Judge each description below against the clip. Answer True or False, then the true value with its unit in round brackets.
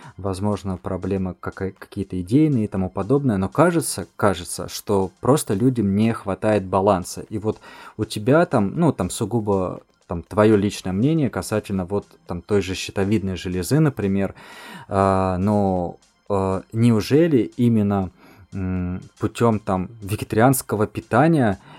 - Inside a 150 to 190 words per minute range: False (120 wpm)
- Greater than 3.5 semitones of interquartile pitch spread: False (2.9 semitones)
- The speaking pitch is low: True (100 Hz)